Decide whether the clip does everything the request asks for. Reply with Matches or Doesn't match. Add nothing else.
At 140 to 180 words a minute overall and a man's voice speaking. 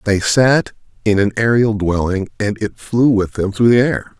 Doesn't match